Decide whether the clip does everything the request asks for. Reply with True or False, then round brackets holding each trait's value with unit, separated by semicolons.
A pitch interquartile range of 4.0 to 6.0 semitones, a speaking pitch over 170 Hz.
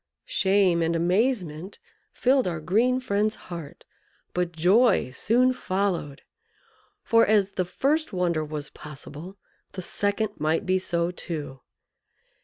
True (4.4 semitones; 185 Hz)